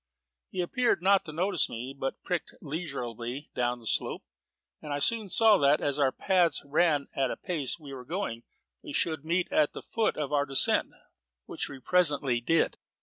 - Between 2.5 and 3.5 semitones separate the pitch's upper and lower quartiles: No, average, 4.8 semitones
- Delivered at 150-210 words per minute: Yes, average, 190 wpm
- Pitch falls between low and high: Yes, medium, 150 Hz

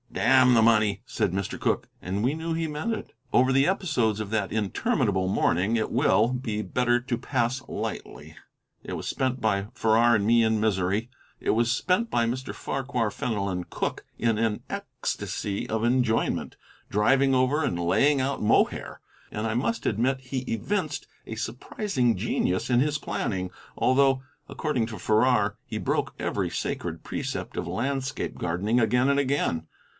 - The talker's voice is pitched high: No, low, 120 Hz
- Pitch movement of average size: Yes, average, 3.8 semitones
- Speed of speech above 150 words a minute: Yes, average, 160 wpm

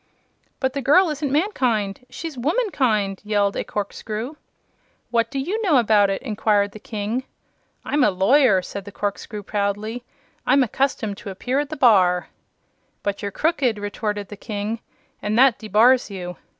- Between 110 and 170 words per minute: Yes, average, 160 wpm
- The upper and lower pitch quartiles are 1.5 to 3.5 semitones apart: No, average, 4.7 semitones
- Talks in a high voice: Yes, high, 220 Hz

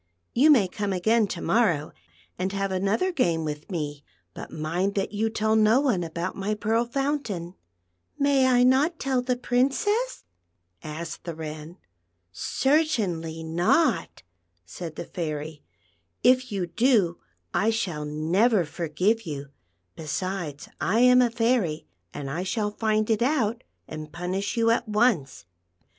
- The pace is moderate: Yes, average, 150 wpm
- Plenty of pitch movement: Yes, wide, 6.8 semitones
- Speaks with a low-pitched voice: No, high, 195 Hz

